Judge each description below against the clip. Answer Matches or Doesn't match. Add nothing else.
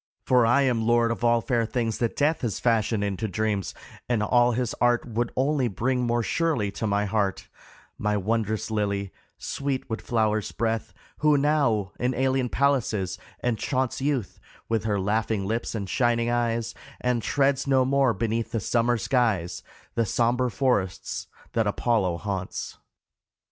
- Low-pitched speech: Matches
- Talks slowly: Doesn't match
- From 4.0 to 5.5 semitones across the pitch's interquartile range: Doesn't match